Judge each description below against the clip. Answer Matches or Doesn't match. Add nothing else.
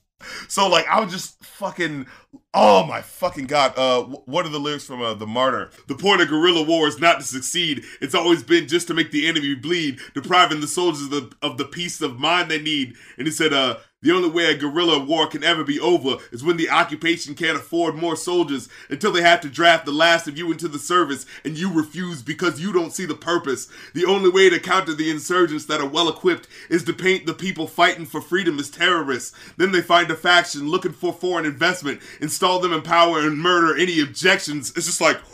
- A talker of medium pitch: Matches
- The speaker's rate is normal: Doesn't match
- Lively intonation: Doesn't match